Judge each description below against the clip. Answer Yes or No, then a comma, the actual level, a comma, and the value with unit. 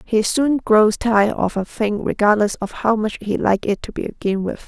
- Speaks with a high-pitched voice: Yes, high, 215 Hz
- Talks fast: Yes, fast, 220 wpm